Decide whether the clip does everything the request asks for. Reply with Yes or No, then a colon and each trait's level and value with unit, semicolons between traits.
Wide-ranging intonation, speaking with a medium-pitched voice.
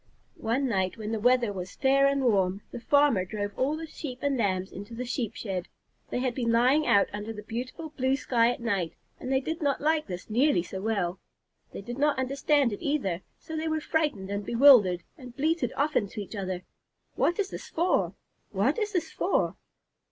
No: wide, 6.0 semitones; high, 245 Hz